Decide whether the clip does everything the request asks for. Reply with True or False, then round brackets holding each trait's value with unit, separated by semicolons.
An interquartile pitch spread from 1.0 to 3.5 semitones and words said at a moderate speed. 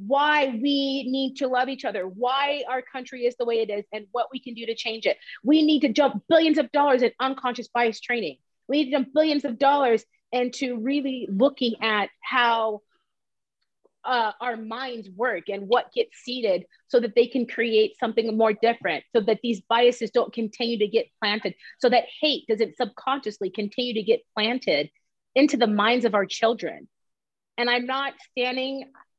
True (3.0 semitones; 185 wpm)